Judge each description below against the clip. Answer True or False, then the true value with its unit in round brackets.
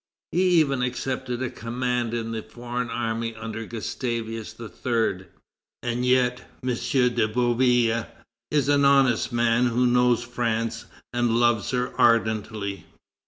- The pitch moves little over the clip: True (1.6 semitones)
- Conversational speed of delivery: False (125 wpm)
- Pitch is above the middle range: False (120 Hz)